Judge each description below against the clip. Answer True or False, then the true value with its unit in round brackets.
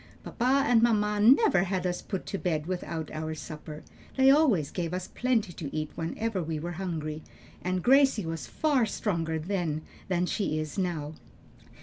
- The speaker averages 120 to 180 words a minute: True (165 wpm)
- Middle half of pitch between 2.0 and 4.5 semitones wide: False (5.3 semitones)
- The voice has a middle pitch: True (180 Hz)